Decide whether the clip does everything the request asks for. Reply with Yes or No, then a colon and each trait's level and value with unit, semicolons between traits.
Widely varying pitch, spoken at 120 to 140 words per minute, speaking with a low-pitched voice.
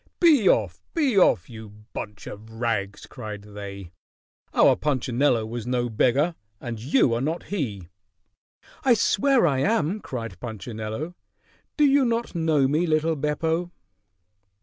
Yes: wide, 7.7 semitones; slow, 135 wpm; low, 130 Hz